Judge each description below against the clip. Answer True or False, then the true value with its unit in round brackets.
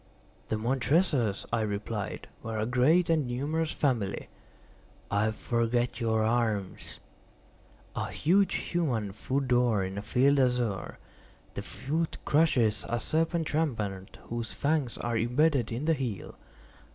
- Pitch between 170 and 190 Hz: False (120 Hz)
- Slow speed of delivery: True (125 wpm)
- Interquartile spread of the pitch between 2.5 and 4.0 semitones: False (4.9 semitones)